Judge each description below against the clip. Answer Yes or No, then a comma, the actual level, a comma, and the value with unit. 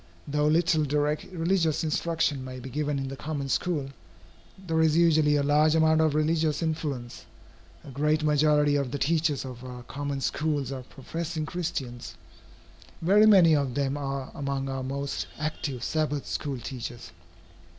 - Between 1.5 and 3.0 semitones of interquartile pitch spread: Yes, narrow, 2.6 semitones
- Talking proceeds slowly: No, average, 155 wpm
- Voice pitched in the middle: Yes, medium, 150 Hz